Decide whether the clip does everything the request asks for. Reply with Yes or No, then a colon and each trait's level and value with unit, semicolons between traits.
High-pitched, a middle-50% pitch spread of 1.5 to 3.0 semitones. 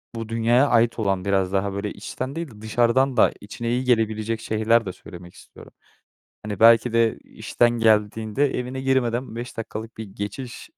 No: low, 115 Hz; narrow, 2.4 semitones